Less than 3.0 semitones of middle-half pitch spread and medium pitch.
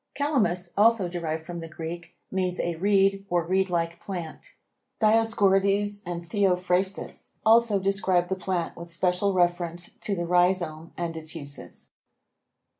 Yes: narrow, 2.4 semitones; medium, 180 Hz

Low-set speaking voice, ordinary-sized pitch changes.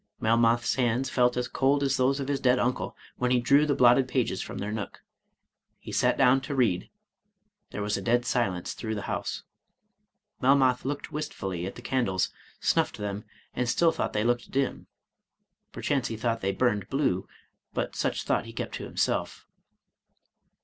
Yes: low, 125 Hz; average, 3.5 semitones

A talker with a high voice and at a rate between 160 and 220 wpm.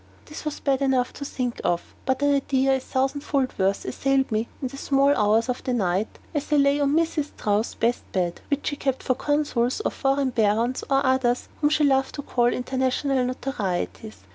Yes: very high, 265 Hz; average, 195 wpm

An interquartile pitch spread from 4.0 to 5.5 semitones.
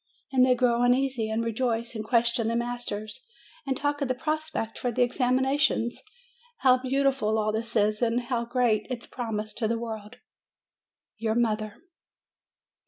No: narrow, 2.5 semitones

